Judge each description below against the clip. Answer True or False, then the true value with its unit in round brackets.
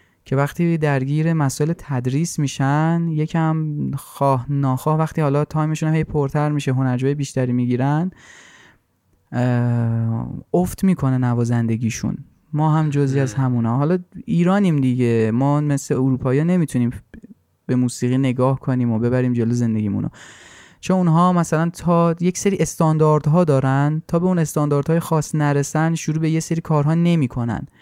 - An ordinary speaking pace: True (135 wpm)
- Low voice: False (145 Hz)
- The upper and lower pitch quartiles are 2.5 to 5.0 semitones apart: True (4.0 semitones)